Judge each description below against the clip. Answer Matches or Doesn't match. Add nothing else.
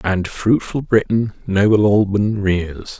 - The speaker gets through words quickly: Doesn't match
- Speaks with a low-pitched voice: Matches